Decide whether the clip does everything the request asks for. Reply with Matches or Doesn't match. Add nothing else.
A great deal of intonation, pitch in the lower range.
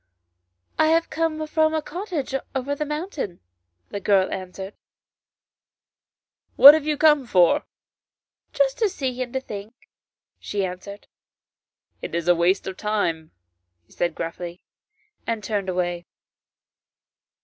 Doesn't match